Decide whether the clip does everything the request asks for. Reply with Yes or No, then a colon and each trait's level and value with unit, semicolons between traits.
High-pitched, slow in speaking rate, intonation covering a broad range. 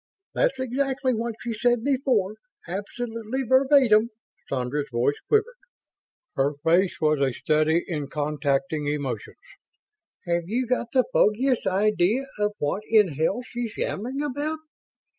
Yes: high, 210 Hz; slow, 125 wpm; wide, 8.6 semitones